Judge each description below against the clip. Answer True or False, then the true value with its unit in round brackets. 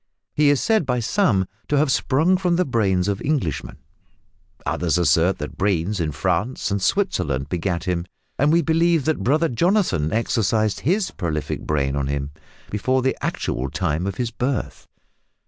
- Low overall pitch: True (110 Hz)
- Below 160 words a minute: False (165 wpm)